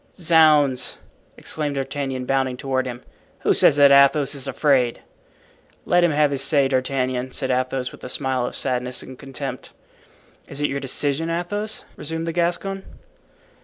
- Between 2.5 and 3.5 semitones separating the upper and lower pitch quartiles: Yes, average, 2.9 semitones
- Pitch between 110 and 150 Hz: Yes, medium, 140 Hz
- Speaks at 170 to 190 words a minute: No, average, 155 wpm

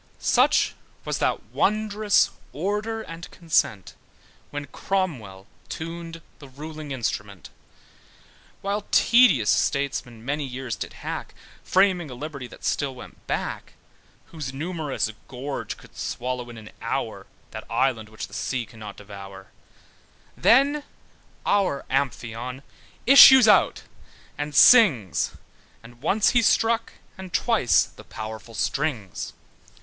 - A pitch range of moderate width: No, wide, 7.9 semitones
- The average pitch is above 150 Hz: No, medium, 140 Hz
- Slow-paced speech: Yes, slow, 115 wpm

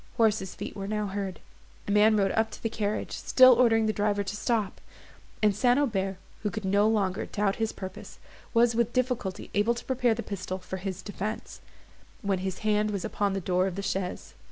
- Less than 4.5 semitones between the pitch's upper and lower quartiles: Yes, narrow, 2.6 semitones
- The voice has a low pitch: No, high, 210 Hz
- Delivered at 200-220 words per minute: Yes, fast, 205 wpm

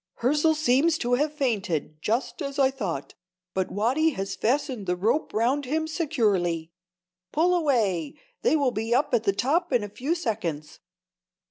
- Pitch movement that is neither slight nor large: No, wide, 6.9 semitones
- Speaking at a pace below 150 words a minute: No, average, 155 wpm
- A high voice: Yes, very high, 250 Hz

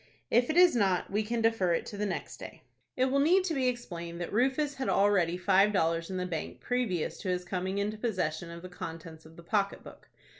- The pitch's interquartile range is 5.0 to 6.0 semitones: Yes, wide, 5.6 semitones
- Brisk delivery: Yes, fast, 230 wpm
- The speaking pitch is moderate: No, high, 195 Hz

